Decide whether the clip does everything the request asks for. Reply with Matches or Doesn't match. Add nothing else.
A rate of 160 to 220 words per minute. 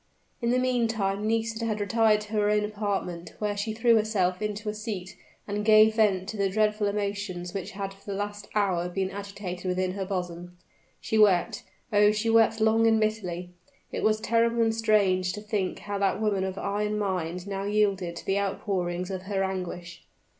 Matches